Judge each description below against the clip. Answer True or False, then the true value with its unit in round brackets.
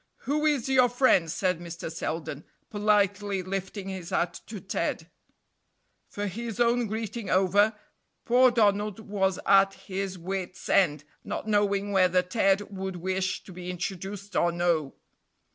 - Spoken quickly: False (140 wpm)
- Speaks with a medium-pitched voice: False (195 Hz)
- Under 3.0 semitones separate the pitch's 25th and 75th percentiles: True (2.5 semitones)